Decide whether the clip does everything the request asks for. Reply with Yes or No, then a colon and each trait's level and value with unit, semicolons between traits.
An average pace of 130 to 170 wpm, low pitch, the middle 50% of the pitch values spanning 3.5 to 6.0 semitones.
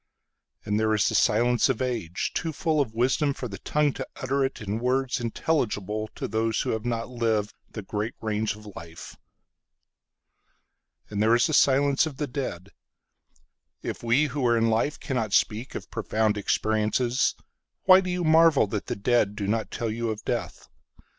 Yes: average, 155 wpm; low, 115 Hz; average, 3.9 semitones